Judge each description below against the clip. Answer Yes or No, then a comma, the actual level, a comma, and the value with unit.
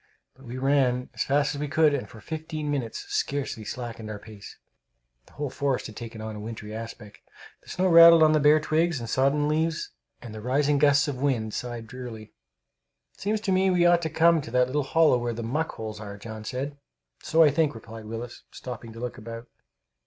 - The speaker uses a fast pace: Yes, fast, 210 wpm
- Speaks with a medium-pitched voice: No, low, 130 Hz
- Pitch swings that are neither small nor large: Yes, average, 4.9 semitones